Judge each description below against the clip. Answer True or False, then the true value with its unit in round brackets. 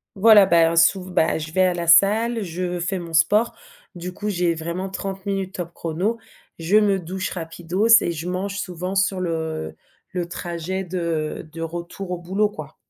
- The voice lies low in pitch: False (180 Hz)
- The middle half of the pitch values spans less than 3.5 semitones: True (2.6 semitones)